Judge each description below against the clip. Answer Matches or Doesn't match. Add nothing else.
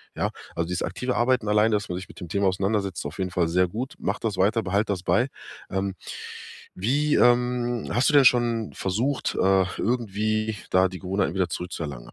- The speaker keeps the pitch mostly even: Doesn't match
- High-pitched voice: Doesn't match